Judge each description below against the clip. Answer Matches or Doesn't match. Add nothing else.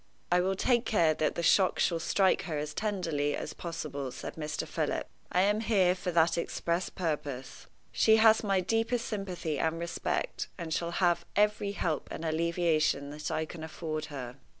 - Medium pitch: Matches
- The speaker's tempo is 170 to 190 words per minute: Matches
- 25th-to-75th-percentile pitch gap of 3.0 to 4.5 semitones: Matches